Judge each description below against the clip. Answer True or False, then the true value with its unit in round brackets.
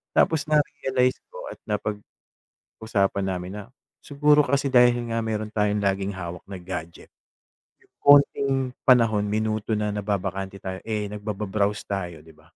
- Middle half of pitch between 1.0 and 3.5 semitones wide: False (4.0 semitones)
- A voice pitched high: False (105 Hz)